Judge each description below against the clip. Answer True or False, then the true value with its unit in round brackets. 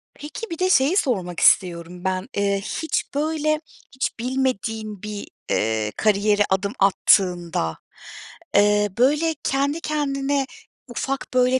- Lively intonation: True (6.4 semitones)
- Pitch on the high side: True (225 Hz)